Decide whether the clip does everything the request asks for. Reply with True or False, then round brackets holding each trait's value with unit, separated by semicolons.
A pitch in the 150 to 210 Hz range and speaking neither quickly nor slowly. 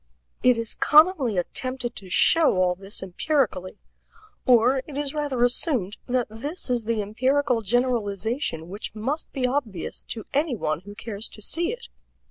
False (240 Hz; 155 wpm)